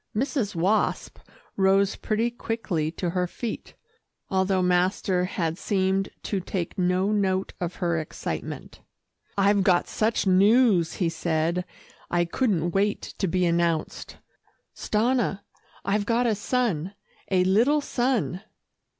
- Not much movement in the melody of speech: No, average, 3.1 semitones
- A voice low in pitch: No, high, 190 Hz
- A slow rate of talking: Yes, slow, 125 wpm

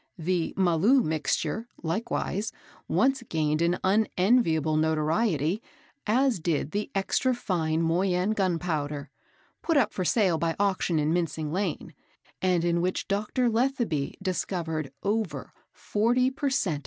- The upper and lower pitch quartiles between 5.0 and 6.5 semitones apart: Yes, wide, 5.4 semitones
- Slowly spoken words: Yes, slow, 125 wpm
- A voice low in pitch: No, medium, 180 Hz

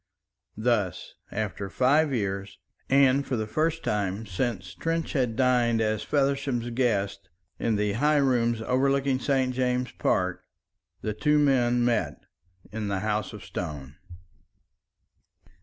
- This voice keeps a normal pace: No, slow, 125 wpm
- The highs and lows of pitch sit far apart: No, average, 4.4 semitones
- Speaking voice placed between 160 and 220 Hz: No, low, 120 Hz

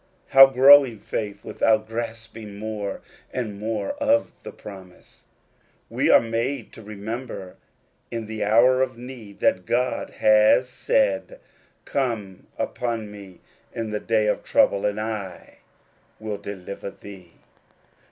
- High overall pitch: No, low, 110 Hz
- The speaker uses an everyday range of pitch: Yes, average, 3.3 semitones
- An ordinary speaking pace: No, slow, 130 wpm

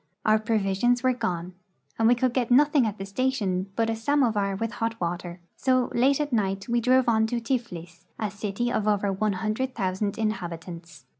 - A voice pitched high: Yes, high, 220 Hz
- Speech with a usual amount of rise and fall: Yes, average, 3.9 semitones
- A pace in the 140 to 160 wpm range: No, average, 190 wpm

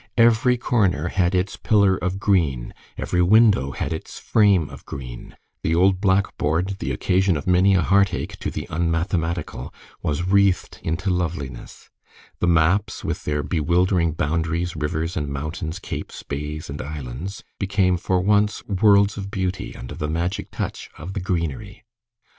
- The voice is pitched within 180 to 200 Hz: No, very low, 90 Hz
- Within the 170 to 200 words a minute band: No, average, 150 wpm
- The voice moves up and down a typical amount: Yes, average, 3.8 semitones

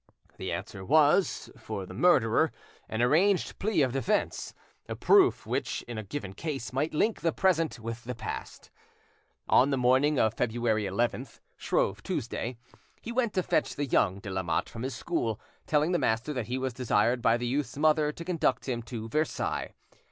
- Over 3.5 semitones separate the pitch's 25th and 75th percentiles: Yes, average, 5.2 semitones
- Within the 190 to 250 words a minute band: No, average, 180 wpm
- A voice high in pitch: No, low, 130 Hz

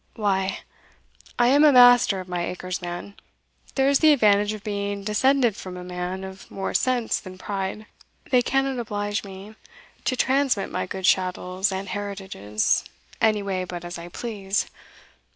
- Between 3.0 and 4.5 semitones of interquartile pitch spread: Yes, average, 4.1 semitones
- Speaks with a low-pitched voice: No, high, 200 Hz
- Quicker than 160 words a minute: No, average, 155 wpm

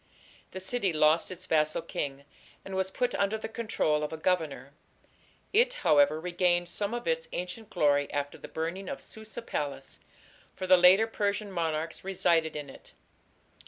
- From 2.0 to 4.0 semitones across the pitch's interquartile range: No, average, 4.9 semitones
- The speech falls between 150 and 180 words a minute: Yes, average, 165 wpm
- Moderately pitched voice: Yes, medium, 180 Hz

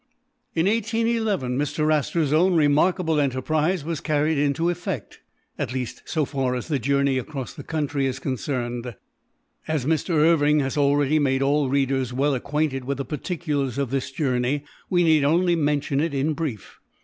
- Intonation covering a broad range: No, average, 3.0 semitones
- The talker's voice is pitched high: No, medium, 145 Hz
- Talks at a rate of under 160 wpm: No, average, 165 wpm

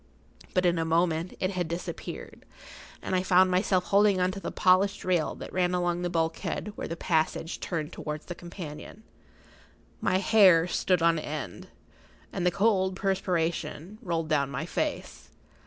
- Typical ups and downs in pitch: No, narrow, 2.3 semitones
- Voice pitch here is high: No, medium, 180 Hz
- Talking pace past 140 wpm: Yes, average, 165 wpm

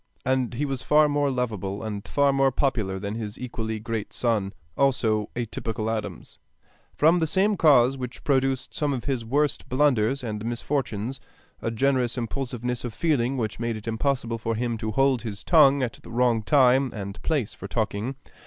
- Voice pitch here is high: No, low, 125 Hz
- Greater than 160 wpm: Yes, average, 180 wpm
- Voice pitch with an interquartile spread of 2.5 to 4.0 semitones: Yes, average, 3.5 semitones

